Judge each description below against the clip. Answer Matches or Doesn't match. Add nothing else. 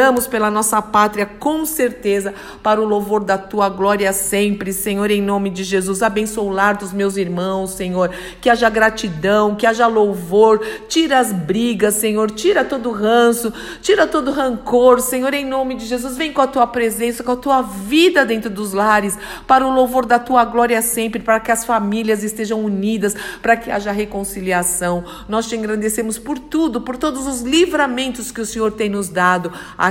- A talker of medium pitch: Doesn't match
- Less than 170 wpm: Doesn't match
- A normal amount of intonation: Matches